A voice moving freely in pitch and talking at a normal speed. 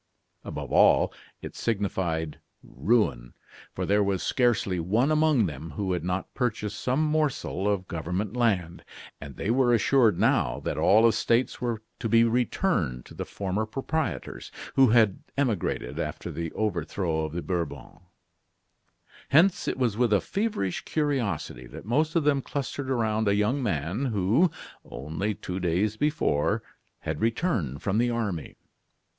Yes: wide, 5.7 semitones; average, 150 wpm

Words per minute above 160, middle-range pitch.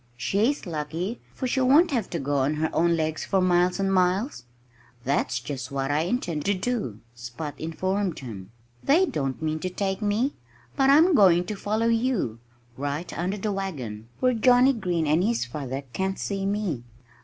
Yes: average, 180 wpm; medium, 180 Hz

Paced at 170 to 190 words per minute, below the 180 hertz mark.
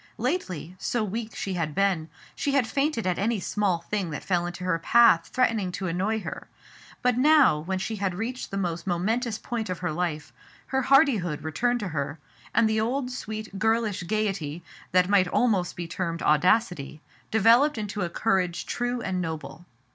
No: average, 175 wpm; high, 195 Hz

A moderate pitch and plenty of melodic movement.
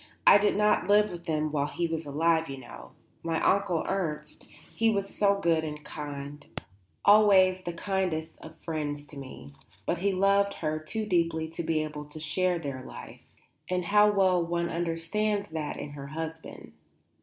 No: medium, 165 Hz; average, 4.0 semitones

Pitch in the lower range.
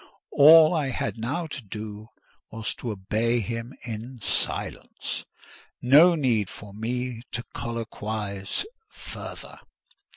Yes: low, 115 Hz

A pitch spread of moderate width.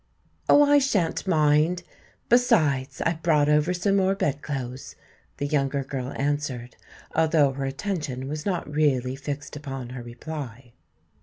Yes: average, 3.8 semitones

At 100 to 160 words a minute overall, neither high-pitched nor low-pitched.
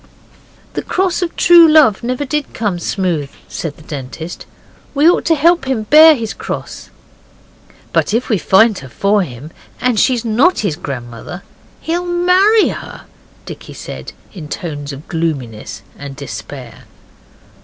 No: average, 150 wpm; high, 210 Hz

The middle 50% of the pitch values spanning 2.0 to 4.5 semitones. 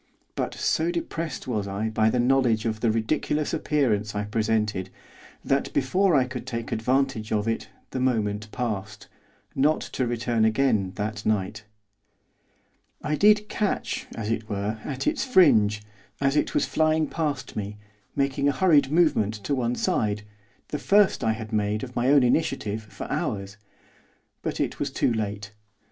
No: average, 4.9 semitones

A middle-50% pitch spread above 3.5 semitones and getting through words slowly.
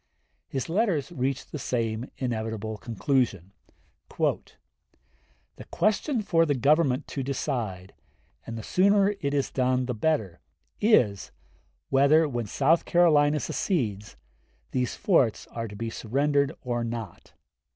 Yes: average, 5.1 semitones; slow, 120 wpm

